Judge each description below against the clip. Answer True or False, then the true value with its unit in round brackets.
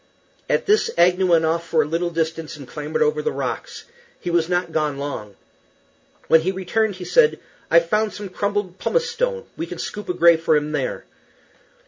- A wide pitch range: False (4.6 semitones)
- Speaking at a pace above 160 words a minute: True (190 wpm)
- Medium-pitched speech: True (175 Hz)